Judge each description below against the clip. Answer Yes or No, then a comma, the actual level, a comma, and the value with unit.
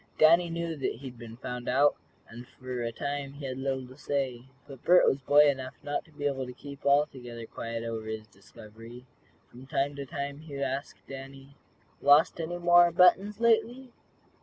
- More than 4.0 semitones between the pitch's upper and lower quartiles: No, average, 3.1 semitones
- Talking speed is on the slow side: No, average, 190 wpm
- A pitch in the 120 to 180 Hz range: Yes, medium, 140 Hz